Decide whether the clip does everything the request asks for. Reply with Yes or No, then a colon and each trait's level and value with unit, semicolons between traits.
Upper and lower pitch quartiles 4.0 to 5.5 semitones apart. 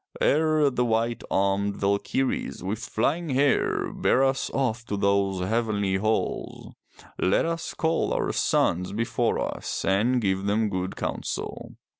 Yes: average, 4.8 semitones